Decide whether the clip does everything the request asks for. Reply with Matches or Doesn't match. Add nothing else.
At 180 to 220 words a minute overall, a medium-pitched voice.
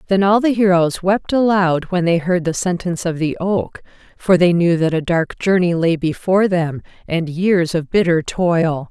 Matches